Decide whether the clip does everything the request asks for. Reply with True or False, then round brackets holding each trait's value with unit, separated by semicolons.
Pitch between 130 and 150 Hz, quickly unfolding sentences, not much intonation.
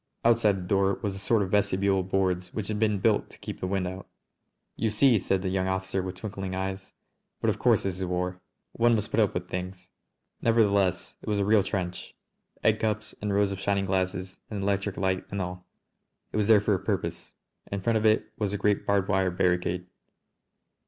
False (95 Hz; 215 wpm; 2.0 semitones)